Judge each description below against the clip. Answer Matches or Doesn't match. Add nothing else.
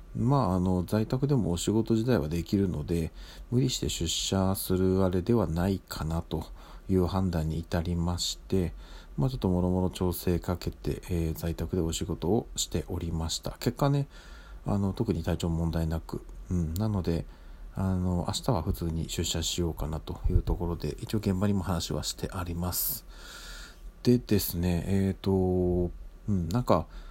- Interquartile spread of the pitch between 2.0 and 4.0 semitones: Matches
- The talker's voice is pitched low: Matches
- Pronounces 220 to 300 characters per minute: Doesn't match